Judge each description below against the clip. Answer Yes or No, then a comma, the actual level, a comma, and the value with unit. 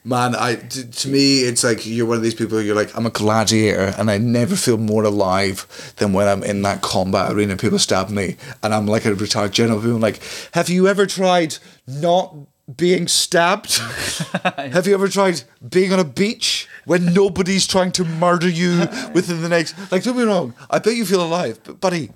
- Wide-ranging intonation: Yes, wide, 8.8 semitones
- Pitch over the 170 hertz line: No, medium, 140 Hz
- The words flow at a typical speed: No, fast, 210 wpm